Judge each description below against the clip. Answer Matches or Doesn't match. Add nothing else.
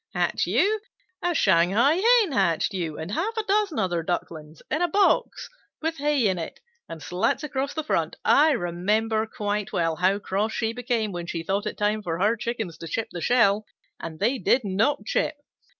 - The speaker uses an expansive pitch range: Matches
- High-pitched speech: Matches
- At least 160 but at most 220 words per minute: Matches